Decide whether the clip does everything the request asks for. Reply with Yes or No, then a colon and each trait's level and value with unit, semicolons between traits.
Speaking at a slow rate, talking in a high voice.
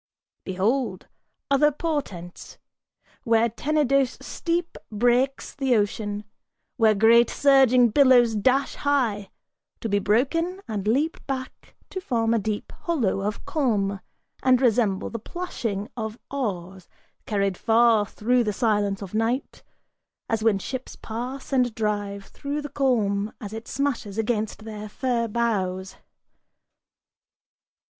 Yes: slow, 120 wpm; high, 230 Hz